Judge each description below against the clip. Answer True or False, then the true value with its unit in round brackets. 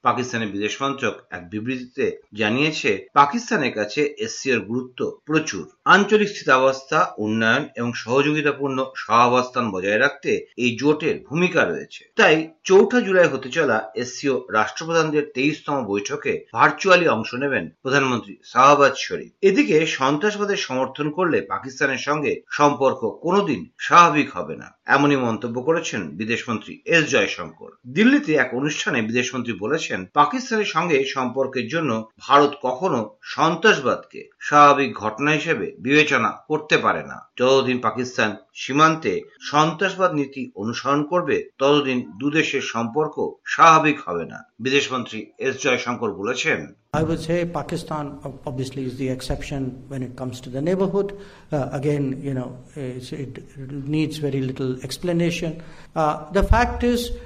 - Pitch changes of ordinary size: True (4.5 semitones)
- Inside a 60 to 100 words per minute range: True (80 wpm)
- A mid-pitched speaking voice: True (145 Hz)